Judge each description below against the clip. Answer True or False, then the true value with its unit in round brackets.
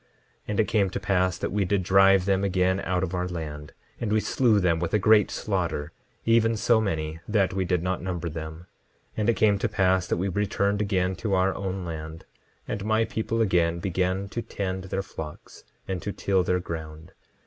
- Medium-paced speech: False (210 wpm)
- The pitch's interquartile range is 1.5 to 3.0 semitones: True (2.6 semitones)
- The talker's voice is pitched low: True (95 Hz)